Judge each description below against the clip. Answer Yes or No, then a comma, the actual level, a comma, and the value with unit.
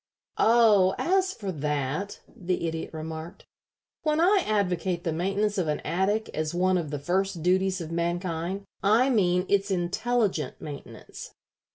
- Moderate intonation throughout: Yes, average, 3.6 semitones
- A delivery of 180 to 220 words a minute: No, average, 145 wpm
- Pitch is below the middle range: No, medium, 185 Hz